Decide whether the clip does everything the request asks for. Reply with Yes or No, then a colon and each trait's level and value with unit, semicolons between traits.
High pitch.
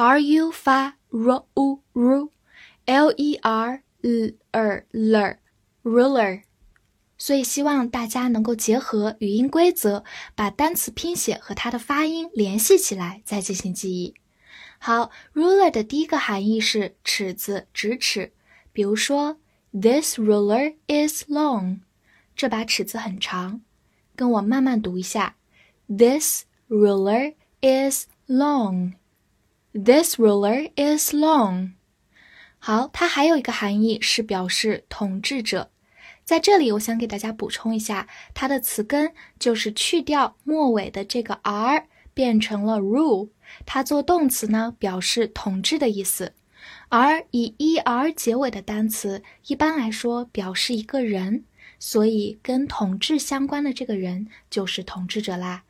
Yes: high, 230 Hz